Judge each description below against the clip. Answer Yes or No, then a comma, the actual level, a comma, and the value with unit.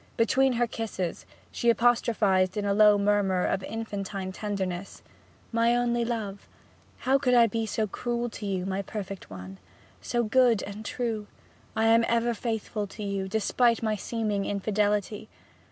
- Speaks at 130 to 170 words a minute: Yes, average, 155 wpm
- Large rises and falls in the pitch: No, average, 2.8 semitones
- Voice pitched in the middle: No, high, 215 Hz